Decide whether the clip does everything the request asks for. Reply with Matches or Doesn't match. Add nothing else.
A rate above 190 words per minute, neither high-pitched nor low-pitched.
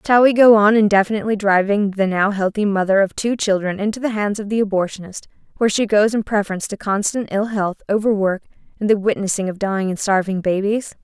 Doesn't match